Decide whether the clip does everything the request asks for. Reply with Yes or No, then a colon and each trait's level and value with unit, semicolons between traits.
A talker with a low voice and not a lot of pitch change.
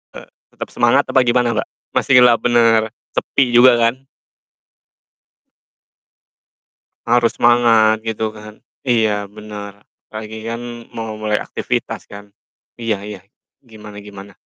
Yes: low, 110 Hz; narrow, 2.1 semitones